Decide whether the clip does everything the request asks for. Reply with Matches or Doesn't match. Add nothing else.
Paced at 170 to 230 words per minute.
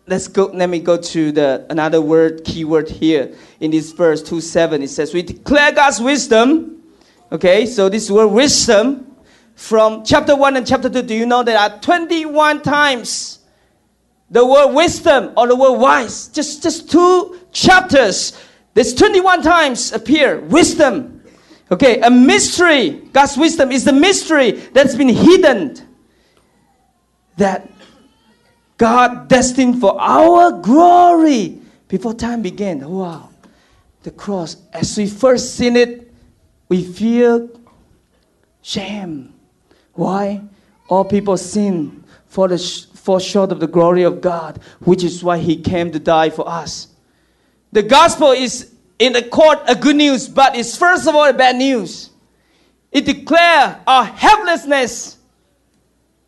Doesn't match